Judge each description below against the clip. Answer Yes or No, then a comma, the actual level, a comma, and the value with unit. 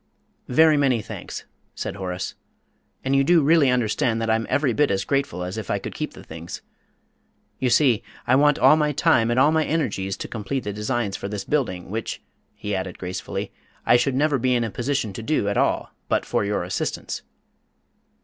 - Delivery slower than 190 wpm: No, average, 195 wpm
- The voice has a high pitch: No, low, 120 Hz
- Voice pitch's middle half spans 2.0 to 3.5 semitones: No, wide, 5.5 semitones